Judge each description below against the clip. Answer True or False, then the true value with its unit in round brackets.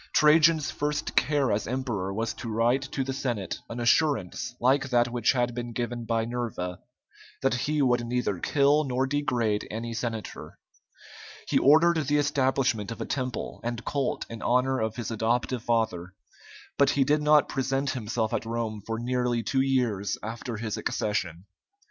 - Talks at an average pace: True (165 wpm)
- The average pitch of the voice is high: False (120 Hz)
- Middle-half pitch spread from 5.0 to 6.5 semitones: False (3.1 semitones)